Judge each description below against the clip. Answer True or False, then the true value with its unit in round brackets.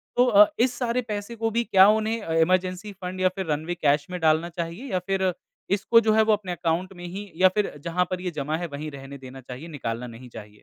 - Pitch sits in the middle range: True (180 Hz)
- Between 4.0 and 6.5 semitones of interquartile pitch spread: True (4.7 semitones)